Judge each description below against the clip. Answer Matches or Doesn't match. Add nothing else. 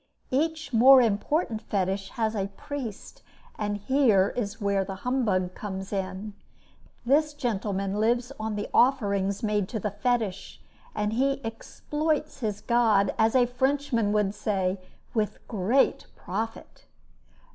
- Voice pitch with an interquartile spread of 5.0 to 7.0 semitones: Doesn't match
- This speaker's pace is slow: Matches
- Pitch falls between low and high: Doesn't match